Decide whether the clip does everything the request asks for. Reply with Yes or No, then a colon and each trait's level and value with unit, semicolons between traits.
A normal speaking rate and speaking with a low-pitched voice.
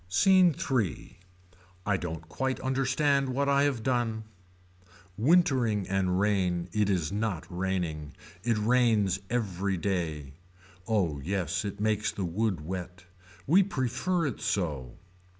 No: slow, 125 wpm; low, 105 Hz